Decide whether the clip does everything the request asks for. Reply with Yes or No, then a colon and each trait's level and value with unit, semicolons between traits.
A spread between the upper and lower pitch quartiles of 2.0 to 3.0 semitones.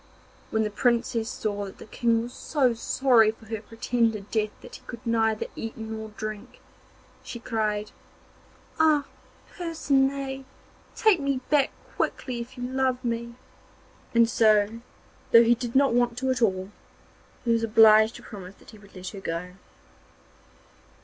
Yes: narrow, 2.6 semitones